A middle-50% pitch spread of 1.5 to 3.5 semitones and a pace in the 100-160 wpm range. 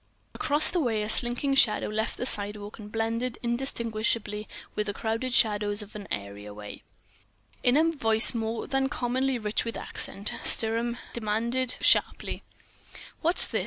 Yes: average, 2.9 semitones; average, 150 wpm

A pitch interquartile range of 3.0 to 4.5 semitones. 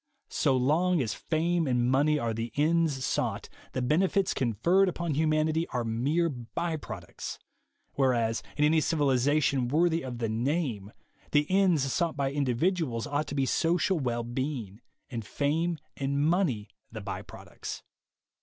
No: average, 5.0 semitones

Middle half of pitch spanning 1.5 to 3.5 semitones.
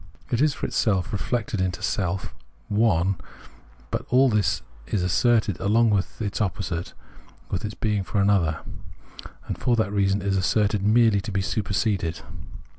Yes: narrow, 2.5 semitones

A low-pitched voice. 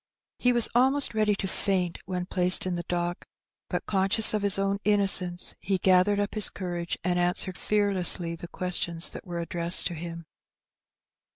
No: medium, 185 Hz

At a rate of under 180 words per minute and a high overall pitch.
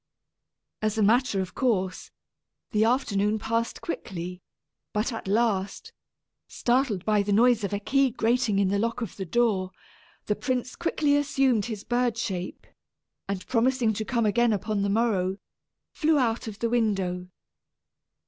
Yes: average, 150 wpm; high, 220 Hz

